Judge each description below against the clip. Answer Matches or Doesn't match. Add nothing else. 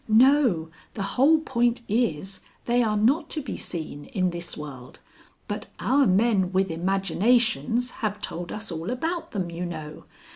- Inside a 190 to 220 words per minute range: Doesn't match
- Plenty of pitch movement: Matches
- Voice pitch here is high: Matches